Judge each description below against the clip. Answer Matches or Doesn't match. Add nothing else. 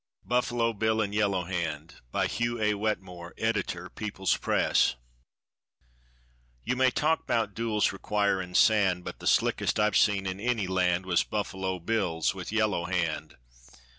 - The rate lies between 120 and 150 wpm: Matches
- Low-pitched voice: Matches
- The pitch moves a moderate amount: Matches